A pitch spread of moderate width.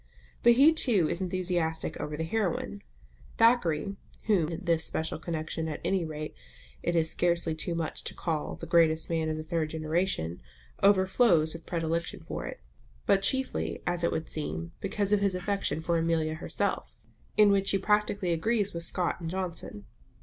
Yes: average, 3.4 semitones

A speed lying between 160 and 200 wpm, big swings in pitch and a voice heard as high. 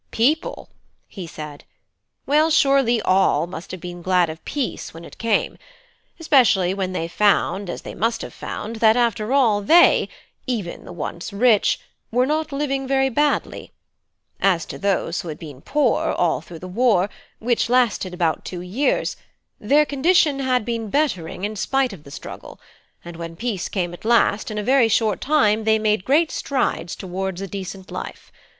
Yes: average, 170 wpm; wide, 6.3 semitones; high, 215 Hz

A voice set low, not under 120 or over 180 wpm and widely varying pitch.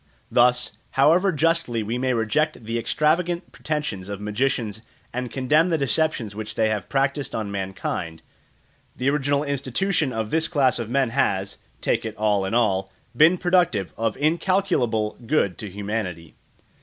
Yes: low, 125 Hz; average, 150 wpm; wide, 6.1 semitones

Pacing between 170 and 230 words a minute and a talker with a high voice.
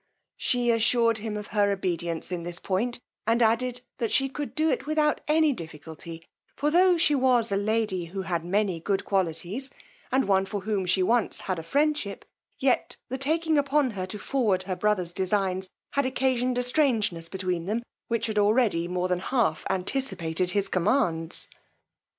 Yes: average, 175 wpm; high, 210 Hz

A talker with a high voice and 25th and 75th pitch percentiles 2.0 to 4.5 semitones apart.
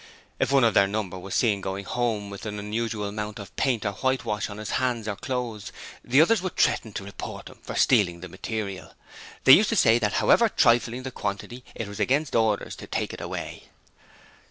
No: low, 110 Hz; average, 3.6 semitones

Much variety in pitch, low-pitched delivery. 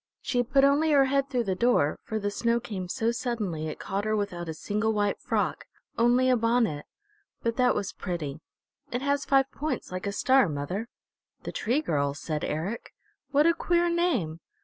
No: wide, 6.5 semitones; high, 230 Hz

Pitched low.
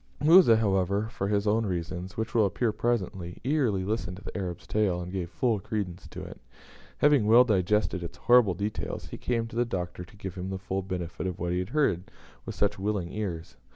Yes: low, 100 Hz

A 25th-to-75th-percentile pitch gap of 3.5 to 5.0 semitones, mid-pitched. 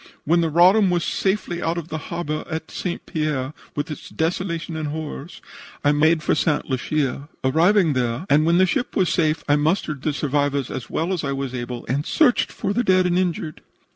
No: average, 3.1 semitones; medium, 155 Hz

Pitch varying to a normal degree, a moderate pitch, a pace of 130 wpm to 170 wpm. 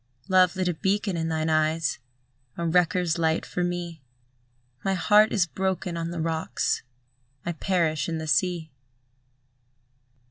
No: narrow, 2.3 semitones; medium, 170 Hz; average, 140 wpm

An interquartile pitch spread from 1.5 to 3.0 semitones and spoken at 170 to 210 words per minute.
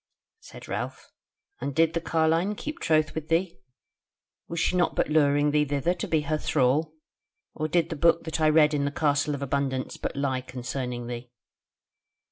Yes: narrow, 2.6 semitones; average, 180 wpm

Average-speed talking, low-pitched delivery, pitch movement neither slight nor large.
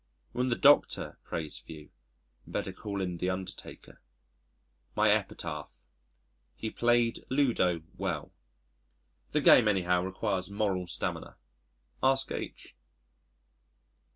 No: slow, 105 wpm; low, 100 Hz; average, 5.0 semitones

